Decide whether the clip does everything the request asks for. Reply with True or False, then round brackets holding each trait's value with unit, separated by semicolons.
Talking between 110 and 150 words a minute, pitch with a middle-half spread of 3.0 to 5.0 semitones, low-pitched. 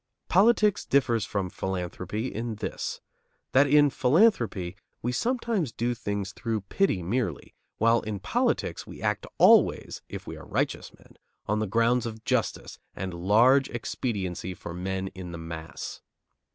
False (140 wpm; 5.4 semitones; 110 Hz)